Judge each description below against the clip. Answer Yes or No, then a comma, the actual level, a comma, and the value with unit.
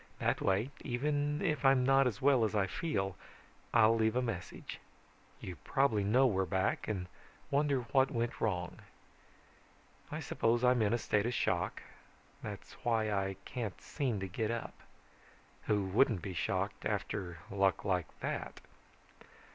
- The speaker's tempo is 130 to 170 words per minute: Yes, average, 150 wpm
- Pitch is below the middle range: Yes, low, 115 Hz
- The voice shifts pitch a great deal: No, average, 4.8 semitones